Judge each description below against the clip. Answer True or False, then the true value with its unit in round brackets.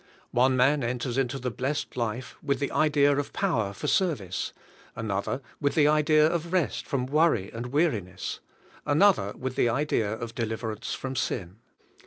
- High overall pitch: False (130 Hz)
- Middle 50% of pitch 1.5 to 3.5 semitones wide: False (4.6 semitones)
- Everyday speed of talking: True (165 wpm)